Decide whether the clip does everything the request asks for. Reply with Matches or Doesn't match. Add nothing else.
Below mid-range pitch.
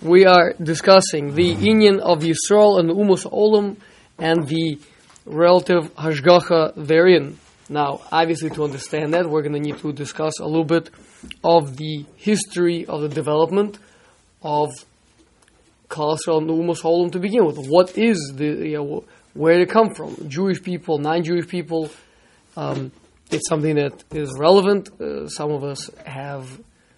Doesn't match